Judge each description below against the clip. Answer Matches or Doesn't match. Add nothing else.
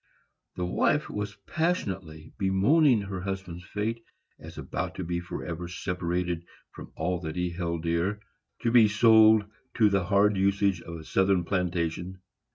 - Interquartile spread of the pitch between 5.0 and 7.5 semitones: Doesn't match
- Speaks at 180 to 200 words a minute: Doesn't match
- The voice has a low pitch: Matches